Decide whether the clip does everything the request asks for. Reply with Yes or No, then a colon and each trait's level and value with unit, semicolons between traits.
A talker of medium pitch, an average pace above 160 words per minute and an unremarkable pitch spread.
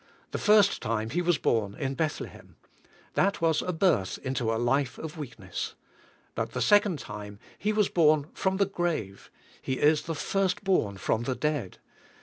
No: medium, 150 Hz; average, 170 wpm; wide, 7.7 semitones